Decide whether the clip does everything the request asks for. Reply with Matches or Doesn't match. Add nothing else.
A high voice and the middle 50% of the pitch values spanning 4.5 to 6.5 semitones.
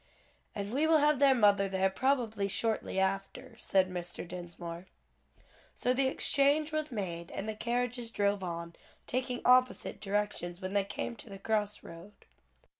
Matches